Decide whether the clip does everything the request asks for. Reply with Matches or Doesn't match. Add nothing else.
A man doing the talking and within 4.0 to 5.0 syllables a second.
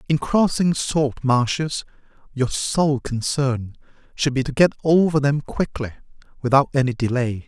Matches